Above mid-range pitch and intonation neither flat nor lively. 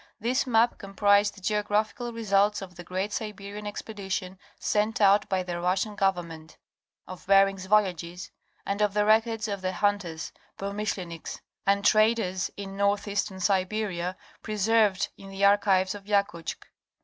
No: high, 200 Hz; narrow, 2.0 semitones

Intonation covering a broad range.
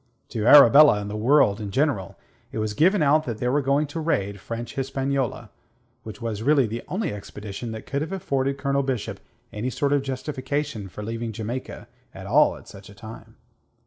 No: average, 4.6 semitones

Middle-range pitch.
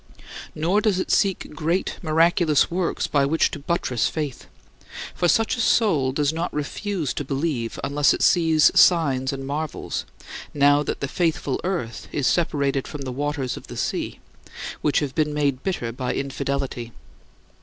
Yes: medium, 150 Hz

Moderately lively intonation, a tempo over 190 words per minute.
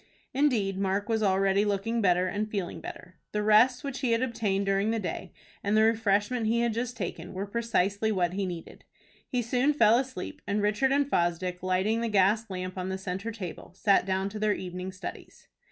Yes: average, 3.3 semitones; average, 200 wpm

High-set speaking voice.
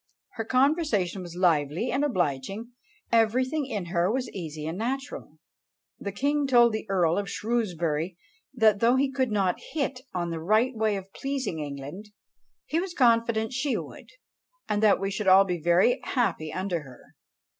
Yes: high, 210 Hz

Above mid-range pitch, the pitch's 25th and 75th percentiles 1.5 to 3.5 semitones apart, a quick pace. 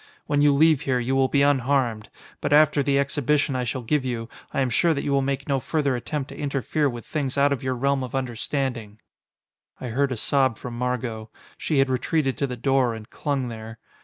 No: low, 135 Hz; narrow, 2.5 semitones; fast, 220 wpm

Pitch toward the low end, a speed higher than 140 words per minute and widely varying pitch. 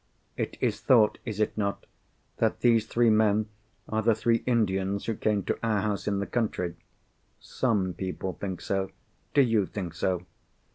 No: low, 105 Hz; average, 155 wpm; average, 2.9 semitones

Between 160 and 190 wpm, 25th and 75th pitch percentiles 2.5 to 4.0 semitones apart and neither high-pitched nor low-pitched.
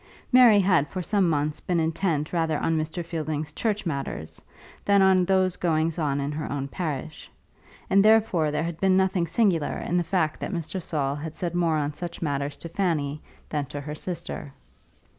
Yes: average, 185 wpm; average, 3.6 semitones; medium, 165 Hz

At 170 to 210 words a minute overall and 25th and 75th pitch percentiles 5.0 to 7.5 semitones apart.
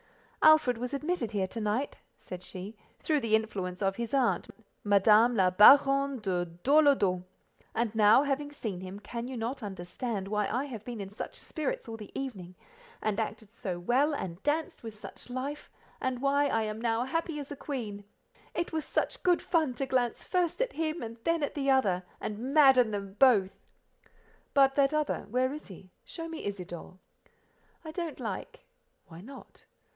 Yes: average, 180 wpm; wide, 5.5 semitones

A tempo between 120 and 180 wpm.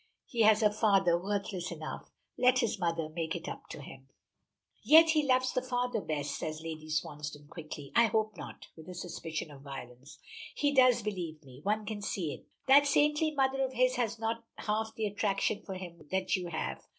No: average, 195 wpm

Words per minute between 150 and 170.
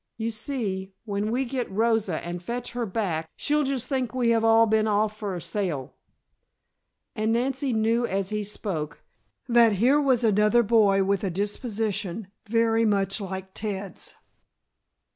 Yes: average, 155 wpm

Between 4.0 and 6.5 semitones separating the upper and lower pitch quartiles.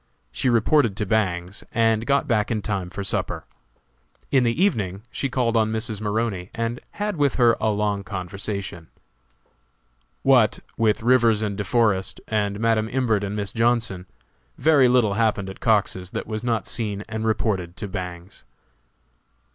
No: average, 2.9 semitones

